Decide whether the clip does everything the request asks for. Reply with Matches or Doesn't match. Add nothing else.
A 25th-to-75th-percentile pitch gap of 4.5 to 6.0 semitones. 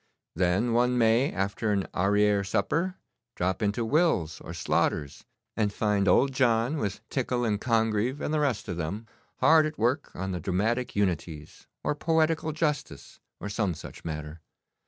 Matches